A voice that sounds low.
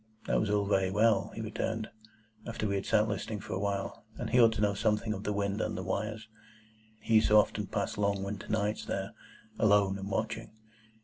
Yes: low, 105 Hz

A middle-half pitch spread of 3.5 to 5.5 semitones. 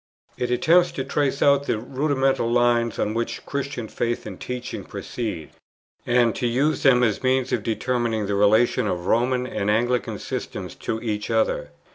No: average, 2.8 semitones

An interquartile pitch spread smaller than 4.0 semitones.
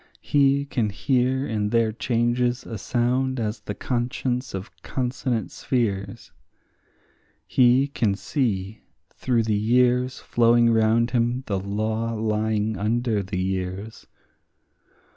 Yes: average, 2.8 semitones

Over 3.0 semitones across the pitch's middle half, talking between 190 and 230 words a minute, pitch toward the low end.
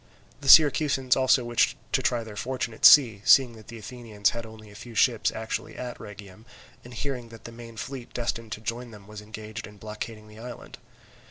No: narrow, 2.4 semitones; average, 200 wpm; low, 115 Hz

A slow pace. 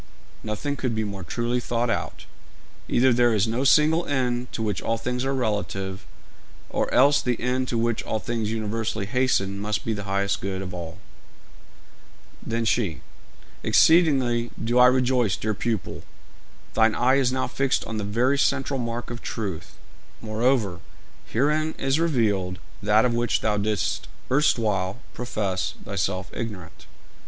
No: average, 150 wpm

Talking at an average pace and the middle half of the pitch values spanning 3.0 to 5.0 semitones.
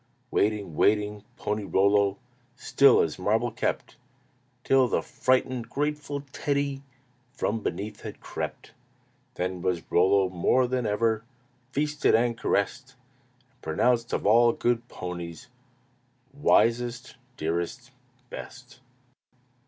No: slow, 105 wpm; average, 4.4 semitones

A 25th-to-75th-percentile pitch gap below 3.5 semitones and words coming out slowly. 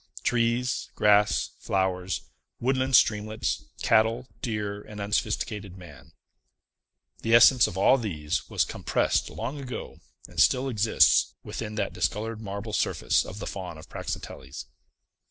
Yes: average, 2.7 semitones; slow, 125 wpm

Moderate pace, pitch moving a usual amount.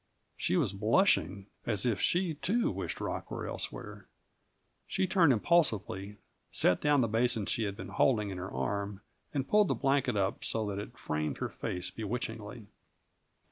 No: average, 160 wpm; wide, 5.9 semitones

